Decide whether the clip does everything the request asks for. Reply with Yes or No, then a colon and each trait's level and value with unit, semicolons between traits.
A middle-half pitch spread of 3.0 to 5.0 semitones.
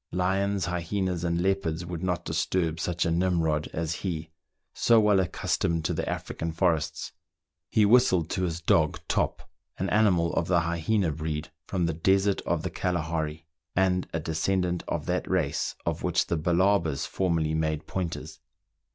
No: narrow, 2.6 semitones